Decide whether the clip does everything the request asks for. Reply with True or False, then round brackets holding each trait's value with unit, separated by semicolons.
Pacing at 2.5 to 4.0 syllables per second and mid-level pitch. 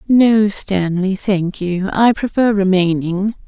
False (3.5 syllables/s; 195 Hz)